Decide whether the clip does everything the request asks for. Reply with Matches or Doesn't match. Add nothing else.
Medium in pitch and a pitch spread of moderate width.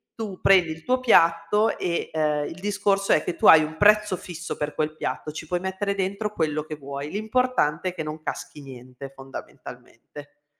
Matches